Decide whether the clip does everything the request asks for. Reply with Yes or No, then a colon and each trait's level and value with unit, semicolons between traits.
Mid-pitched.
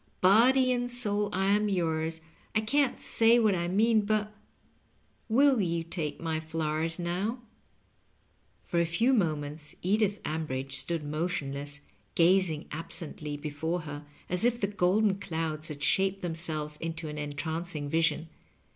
Yes: medium, 170 Hz